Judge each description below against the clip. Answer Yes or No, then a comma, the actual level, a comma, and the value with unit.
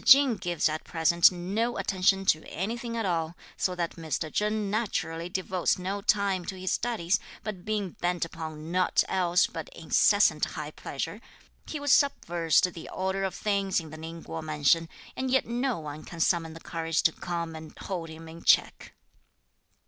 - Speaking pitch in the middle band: Yes, medium, 180 Hz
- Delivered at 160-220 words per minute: Yes, average, 175 wpm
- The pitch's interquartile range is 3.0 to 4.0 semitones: Yes, average, 3.5 semitones